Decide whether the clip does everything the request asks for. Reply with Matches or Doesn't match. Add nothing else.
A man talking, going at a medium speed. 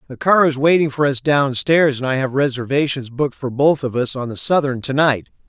Doesn't match